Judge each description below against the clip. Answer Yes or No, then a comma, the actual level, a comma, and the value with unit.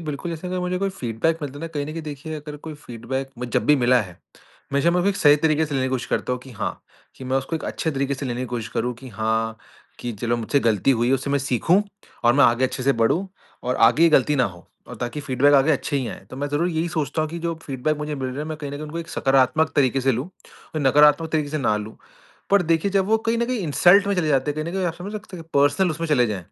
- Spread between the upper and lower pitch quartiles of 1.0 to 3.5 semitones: No, average, 4.2 semitones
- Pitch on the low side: No, medium, 145 Hz